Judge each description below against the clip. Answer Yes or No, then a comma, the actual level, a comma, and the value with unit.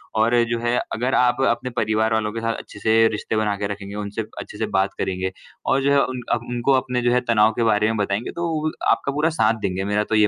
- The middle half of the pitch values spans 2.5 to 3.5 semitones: Yes, average, 2.8 semitones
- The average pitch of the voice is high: No, low, 110 Hz